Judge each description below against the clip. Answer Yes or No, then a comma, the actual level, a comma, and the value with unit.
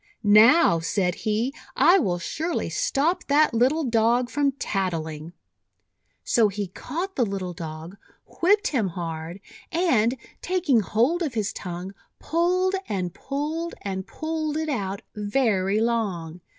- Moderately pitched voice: No, high, 225 Hz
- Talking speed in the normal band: No, slow, 130 wpm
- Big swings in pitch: Yes, wide, 8.4 semitones